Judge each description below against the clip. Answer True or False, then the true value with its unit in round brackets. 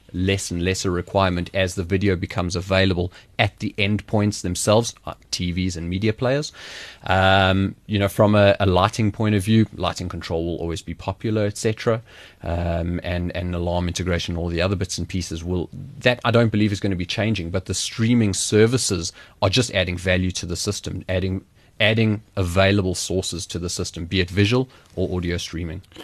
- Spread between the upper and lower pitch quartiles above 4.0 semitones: False (3.0 semitones)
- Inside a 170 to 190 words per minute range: True (180 wpm)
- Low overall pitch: True (95 Hz)